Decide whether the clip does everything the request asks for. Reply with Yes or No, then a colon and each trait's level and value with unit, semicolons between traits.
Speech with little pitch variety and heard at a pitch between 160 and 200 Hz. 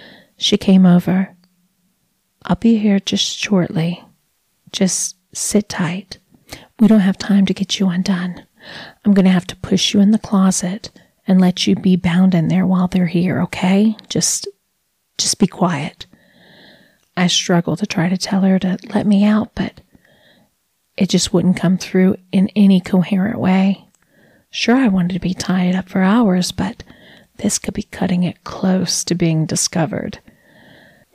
Yes: narrow, 1.9 semitones; high, 190 Hz